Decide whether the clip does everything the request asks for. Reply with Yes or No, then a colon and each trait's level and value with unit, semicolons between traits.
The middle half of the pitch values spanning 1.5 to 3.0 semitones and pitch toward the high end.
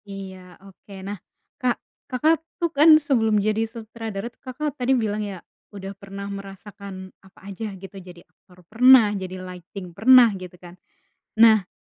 No: average, 3.6 semitones; high, 200 Hz